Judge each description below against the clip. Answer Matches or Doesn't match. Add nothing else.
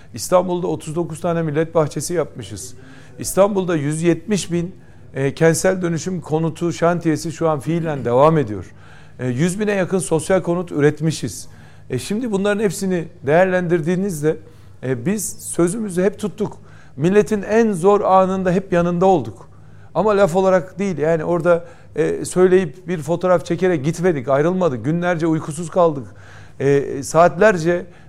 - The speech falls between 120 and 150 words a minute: Matches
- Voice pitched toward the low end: Doesn't match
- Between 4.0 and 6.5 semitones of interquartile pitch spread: Doesn't match